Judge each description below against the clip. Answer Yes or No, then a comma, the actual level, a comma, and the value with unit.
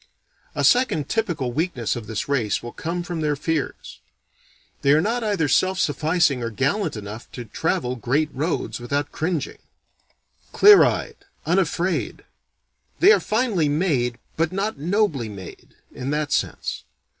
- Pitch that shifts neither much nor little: No, wide, 6.3 semitones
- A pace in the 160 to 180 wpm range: No, average, 145 wpm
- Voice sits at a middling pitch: Yes, medium, 150 Hz